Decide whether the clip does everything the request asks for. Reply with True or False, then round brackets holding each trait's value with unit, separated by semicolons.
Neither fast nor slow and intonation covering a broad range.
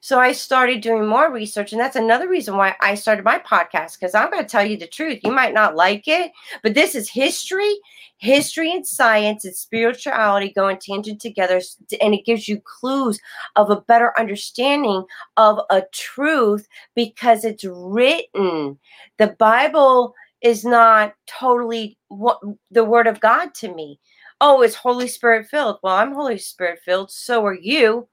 False (170 wpm; 3.6 semitones)